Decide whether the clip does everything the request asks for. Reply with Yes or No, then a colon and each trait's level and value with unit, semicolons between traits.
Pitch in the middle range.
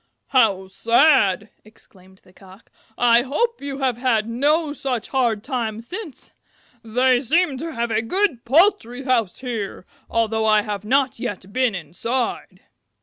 No: high, 235 Hz